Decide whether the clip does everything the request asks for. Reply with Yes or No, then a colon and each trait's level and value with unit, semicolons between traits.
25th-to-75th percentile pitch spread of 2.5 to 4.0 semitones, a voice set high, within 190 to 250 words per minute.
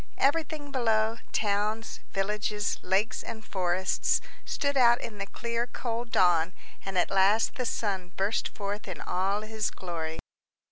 No: average, 3.2 semitones; high, 210 Hz; average, 140 wpm